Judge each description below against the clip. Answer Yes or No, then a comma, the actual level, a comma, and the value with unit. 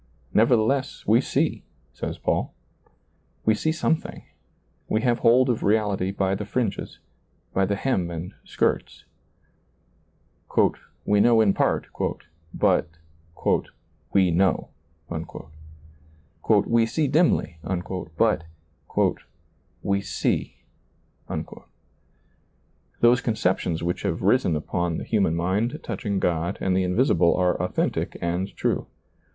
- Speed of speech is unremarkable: No, slow, 115 wpm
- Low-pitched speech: Yes, very low, 95 Hz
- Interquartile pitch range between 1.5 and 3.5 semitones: No, average, 4.9 semitones